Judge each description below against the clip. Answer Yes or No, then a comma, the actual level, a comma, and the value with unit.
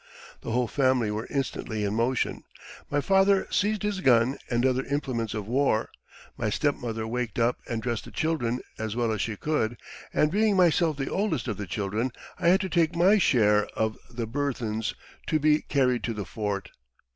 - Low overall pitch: Yes, low, 125 Hz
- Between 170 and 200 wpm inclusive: Yes, average, 185 wpm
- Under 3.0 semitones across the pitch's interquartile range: No, wide, 5.6 semitones